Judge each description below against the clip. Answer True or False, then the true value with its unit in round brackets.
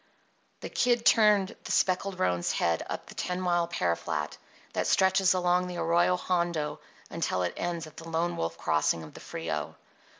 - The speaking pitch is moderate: True (175 Hz)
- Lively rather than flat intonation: False (3.7 semitones)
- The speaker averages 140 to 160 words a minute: False (175 wpm)